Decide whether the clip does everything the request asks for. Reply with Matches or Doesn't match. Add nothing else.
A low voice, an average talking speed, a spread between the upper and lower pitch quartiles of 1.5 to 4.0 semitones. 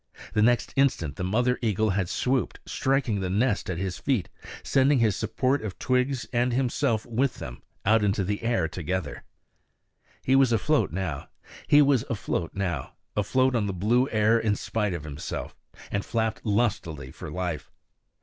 Doesn't match